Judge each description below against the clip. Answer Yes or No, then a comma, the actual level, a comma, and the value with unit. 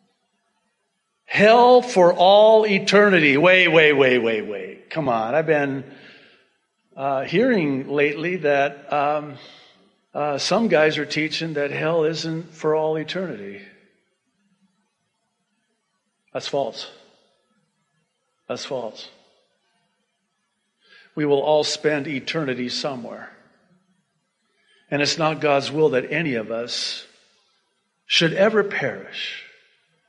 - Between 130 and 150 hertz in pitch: No, medium, 165 Hz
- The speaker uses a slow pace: Yes, slow, 100 wpm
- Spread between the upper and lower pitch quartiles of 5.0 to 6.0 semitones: Yes, wide, 5.6 semitones